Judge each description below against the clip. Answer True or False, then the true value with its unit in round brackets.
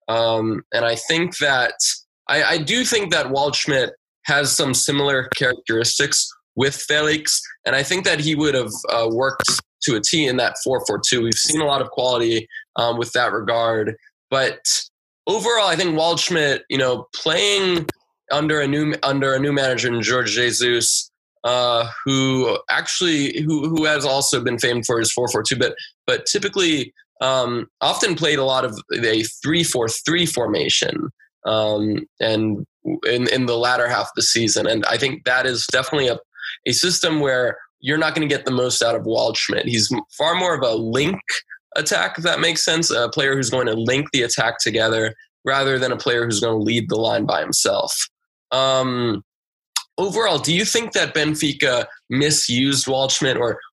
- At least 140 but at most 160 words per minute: False (180 wpm)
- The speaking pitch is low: True (130 Hz)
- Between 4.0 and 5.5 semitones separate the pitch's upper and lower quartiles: True (4.5 semitones)